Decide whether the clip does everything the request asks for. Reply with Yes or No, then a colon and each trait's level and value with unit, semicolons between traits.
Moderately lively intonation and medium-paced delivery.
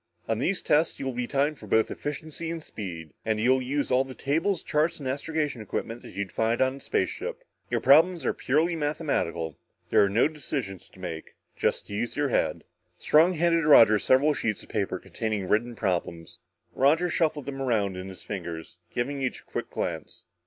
No: wide, 6.5 semitones; average, 190 wpm